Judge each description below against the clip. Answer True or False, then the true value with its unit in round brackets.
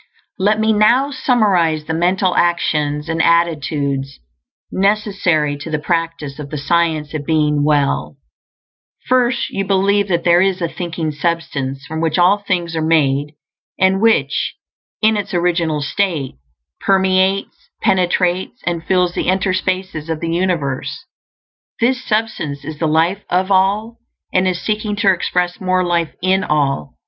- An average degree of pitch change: True (3.9 semitones)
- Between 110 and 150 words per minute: True (145 wpm)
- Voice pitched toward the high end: False (175 Hz)